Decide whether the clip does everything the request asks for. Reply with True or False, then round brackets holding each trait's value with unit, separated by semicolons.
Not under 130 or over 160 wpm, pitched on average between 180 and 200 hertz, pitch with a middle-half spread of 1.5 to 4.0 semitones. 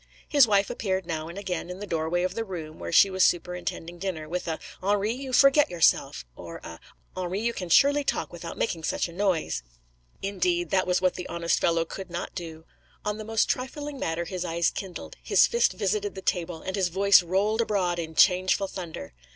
False (205 wpm; 185 Hz; 3.2 semitones)